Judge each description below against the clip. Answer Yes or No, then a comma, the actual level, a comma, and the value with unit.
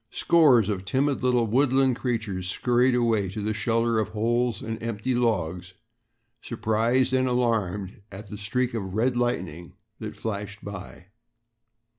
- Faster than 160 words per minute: No, average, 140 wpm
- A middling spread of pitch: Yes, average, 3.5 semitones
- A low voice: Yes, low, 115 Hz